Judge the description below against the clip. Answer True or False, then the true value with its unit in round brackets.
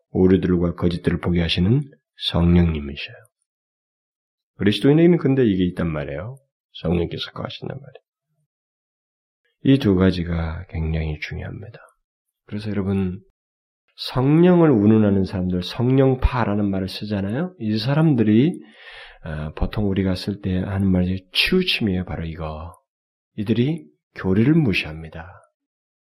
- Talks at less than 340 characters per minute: True (290 characters per minute)